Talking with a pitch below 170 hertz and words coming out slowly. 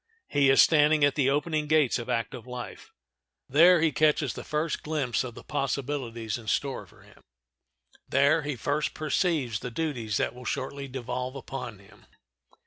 No: medium, 140 Hz; average, 165 wpm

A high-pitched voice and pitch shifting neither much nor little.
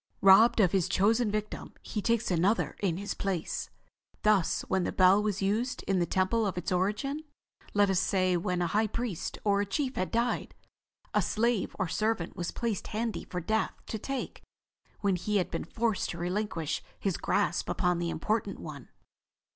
Yes: high, 200 Hz; average, 3.3 semitones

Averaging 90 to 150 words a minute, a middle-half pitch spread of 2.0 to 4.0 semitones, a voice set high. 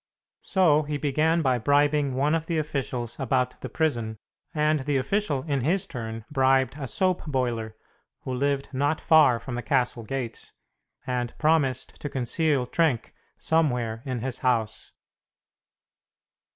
No: average, 140 wpm; average, 3.6 semitones; low, 135 Hz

